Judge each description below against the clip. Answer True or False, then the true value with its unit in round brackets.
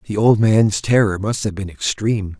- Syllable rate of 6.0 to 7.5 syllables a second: False (5.0 syllables/s)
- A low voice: True (105 Hz)